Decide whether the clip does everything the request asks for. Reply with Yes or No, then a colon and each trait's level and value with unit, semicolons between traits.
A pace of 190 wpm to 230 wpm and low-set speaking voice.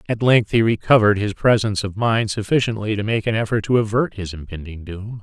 Yes: fast, 205 wpm; low, 105 Hz